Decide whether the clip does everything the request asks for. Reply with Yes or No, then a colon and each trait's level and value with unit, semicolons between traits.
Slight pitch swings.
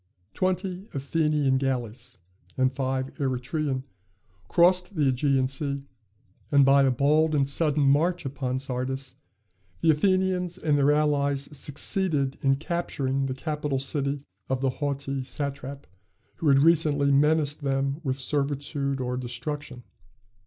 Yes: narrow, 2.2 semitones